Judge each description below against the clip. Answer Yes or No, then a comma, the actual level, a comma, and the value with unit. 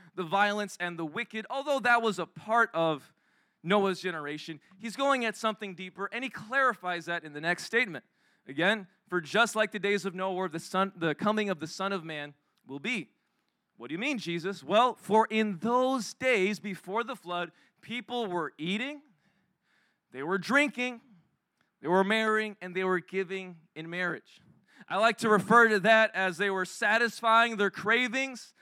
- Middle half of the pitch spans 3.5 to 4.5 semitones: Yes, average, 4.2 semitones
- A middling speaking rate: Yes, average, 180 wpm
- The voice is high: Yes, high, 200 Hz